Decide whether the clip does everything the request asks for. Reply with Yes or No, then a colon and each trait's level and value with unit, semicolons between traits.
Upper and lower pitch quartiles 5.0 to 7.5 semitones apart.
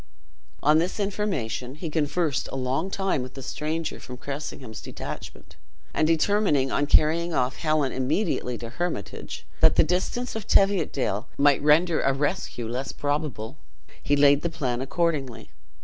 No: average, 4.4 semitones